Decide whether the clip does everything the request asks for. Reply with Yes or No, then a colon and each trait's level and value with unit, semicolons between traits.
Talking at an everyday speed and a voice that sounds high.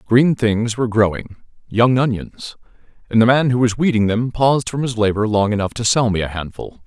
No: average, 190 wpm; low, 115 Hz